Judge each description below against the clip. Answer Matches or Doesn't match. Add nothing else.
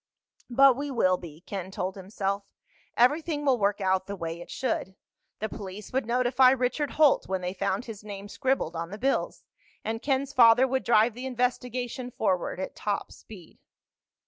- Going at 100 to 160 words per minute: Doesn't match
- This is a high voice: Matches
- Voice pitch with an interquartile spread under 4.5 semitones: Doesn't match